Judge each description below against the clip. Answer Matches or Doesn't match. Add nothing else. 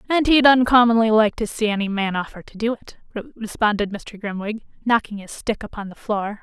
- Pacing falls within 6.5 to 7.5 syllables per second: Doesn't match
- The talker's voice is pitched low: Doesn't match